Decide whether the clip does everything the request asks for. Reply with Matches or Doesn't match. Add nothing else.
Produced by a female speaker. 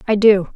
Matches